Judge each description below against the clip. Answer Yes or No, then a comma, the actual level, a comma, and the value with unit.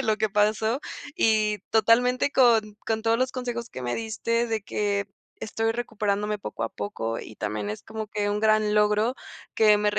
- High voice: Yes, high, 215 Hz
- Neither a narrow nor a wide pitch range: No, narrow, 1.6 semitones